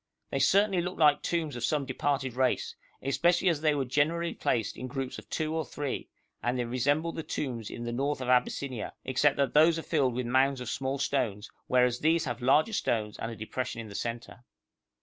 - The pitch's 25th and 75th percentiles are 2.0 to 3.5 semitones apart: No, average, 3.9 semitones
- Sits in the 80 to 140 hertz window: Yes, low, 135 Hz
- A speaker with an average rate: No, fast, 210 wpm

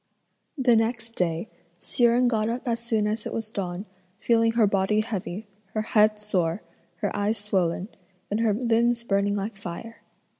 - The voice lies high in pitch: Yes, high, 215 Hz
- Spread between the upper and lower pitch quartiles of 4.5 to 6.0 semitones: No, narrow, 2.4 semitones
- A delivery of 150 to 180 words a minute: Yes, average, 165 wpm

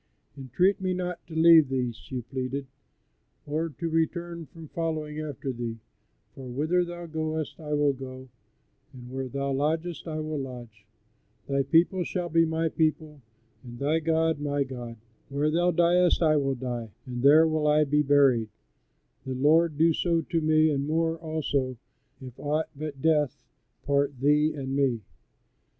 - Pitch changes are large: No, average, 3.3 semitones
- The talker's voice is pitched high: No, medium, 150 Hz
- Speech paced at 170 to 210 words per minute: No, average, 160 wpm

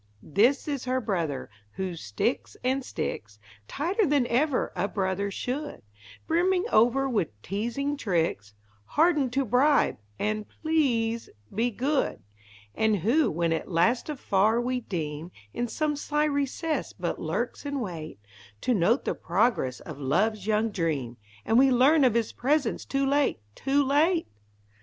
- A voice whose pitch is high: Yes, high, 240 Hz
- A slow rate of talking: No, average, 145 wpm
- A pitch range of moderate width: No, wide, 6.8 semitones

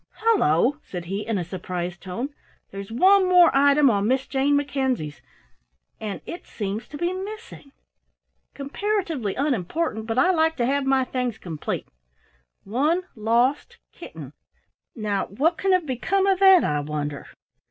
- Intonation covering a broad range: Yes, wide, 8.4 semitones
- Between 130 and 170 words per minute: Yes, average, 145 wpm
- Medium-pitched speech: No, very high, 265 Hz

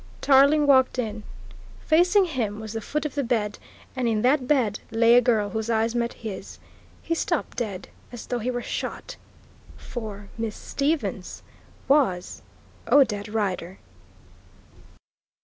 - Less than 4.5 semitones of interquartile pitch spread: Yes, average, 4.1 semitones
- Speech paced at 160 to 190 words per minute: No, average, 140 wpm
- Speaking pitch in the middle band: No, high, 235 Hz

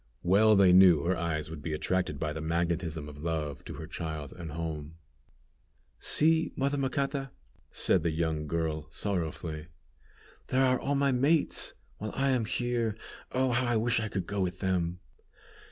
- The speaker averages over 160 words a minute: Yes, average, 170 wpm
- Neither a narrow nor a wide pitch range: No, wide, 7.2 semitones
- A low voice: Yes, very low, 90 Hz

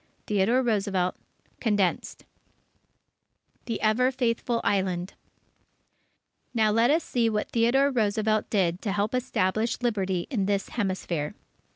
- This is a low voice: No, high, 215 Hz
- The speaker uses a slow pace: Yes, slow, 110 wpm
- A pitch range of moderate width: Yes, average, 3.5 semitones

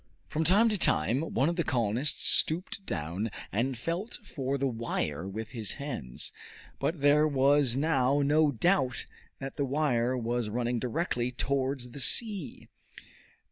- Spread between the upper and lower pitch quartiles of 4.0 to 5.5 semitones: Yes, average, 4.3 semitones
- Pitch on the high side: No, low, 135 Hz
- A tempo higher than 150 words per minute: No, average, 145 wpm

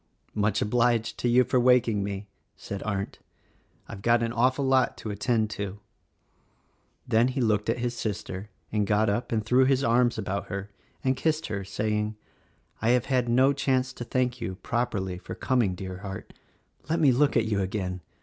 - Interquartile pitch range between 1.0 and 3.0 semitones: No, average, 3.7 semitones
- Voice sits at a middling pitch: No, low, 115 Hz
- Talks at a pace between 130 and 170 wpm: No, average, 180 wpm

